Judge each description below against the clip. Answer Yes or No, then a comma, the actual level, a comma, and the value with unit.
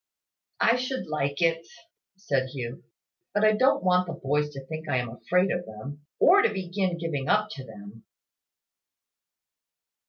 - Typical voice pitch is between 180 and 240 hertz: No, medium, 160 Hz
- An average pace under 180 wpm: Yes, average, 155 wpm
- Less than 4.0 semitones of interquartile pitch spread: No, wide, 5.6 semitones